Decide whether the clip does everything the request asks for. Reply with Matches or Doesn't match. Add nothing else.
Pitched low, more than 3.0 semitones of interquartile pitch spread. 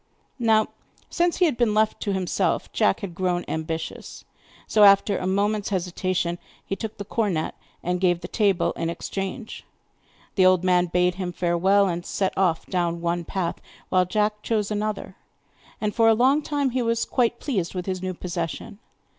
Doesn't match